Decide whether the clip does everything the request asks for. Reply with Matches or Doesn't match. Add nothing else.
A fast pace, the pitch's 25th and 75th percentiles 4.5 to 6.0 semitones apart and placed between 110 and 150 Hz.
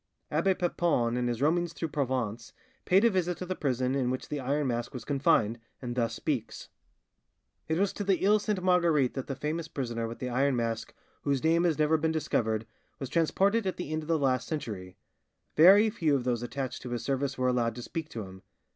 Matches